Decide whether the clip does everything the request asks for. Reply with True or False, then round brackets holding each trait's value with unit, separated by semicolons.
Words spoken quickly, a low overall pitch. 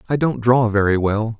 True (215 wpm; 115 Hz)